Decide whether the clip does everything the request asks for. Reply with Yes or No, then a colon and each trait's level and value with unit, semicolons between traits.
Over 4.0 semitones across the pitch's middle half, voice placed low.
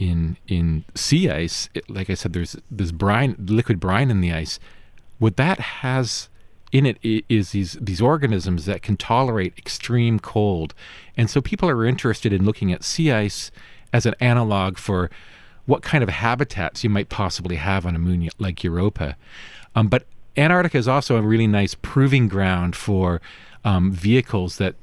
Yes: average, 4.5 semitones; low, 100 Hz